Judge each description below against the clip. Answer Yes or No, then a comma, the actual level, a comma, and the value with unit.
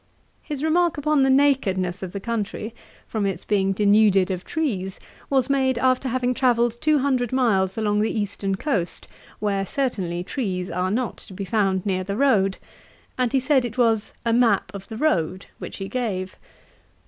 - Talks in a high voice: Yes, high, 220 Hz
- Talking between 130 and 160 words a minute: No, average, 175 wpm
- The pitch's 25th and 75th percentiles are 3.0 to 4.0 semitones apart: No, average, 5.1 semitones